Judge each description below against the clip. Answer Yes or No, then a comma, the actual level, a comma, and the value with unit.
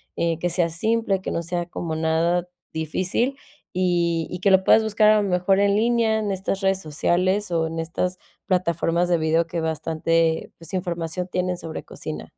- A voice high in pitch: No, medium, 175 Hz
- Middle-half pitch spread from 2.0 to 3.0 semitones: Yes, average, 2.7 semitones